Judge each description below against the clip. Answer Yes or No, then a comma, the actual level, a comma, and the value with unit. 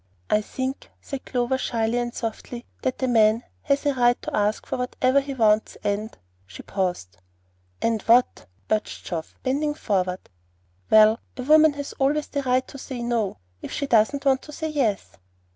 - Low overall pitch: No, high, 245 Hz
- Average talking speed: Yes, average, 175 wpm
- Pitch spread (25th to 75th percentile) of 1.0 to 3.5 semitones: No, average, 4.2 semitones